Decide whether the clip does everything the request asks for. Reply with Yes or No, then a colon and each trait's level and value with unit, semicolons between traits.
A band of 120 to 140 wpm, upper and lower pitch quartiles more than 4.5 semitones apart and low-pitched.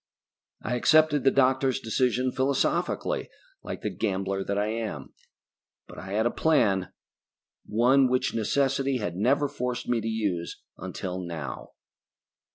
Yes: slow, 135 wpm; average, 5.0 semitones; low, 120 Hz